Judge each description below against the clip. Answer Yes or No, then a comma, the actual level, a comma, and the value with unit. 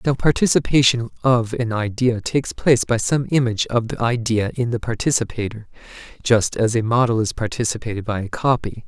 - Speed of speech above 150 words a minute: Yes, average, 170 wpm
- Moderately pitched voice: No, low, 120 Hz